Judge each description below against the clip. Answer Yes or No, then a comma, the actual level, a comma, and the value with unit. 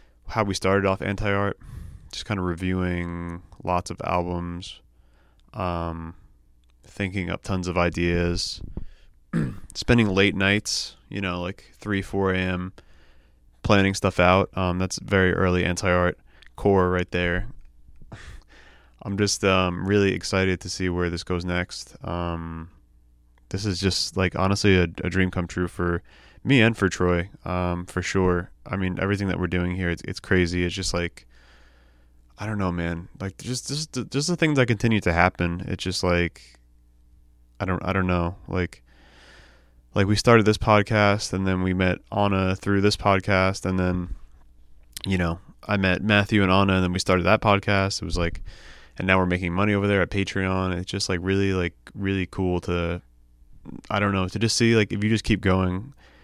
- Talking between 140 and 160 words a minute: No, average, 175 wpm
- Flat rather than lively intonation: Yes, narrow, 2.3 semitones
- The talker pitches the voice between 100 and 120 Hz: No, very low, 90 Hz